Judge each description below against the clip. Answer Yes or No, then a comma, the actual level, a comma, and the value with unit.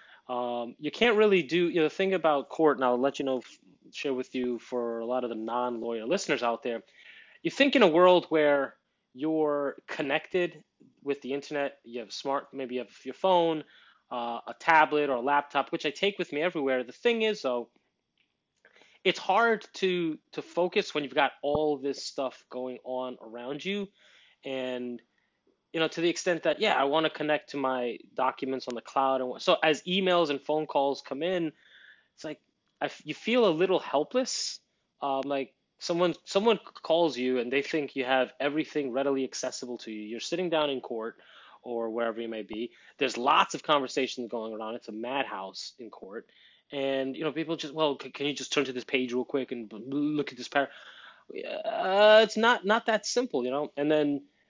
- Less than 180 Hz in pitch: Yes, medium, 140 Hz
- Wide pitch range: No, average, 4.8 semitones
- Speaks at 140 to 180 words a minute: No, average, 200 wpm